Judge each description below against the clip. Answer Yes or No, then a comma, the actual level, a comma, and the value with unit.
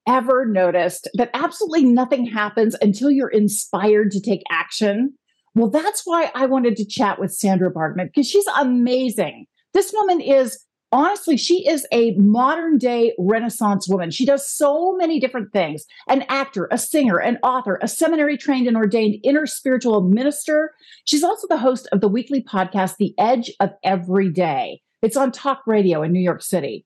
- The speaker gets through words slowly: No, average, 170 wpm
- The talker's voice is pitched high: Yes, high, 245 Hz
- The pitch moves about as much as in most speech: No, wide, 5.8 semitones